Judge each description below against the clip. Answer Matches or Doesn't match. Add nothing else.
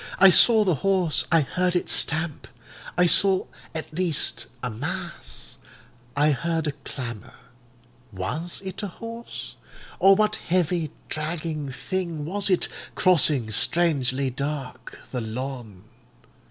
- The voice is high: Doesn't match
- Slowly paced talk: Matches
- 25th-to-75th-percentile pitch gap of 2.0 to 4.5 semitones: Doesn't match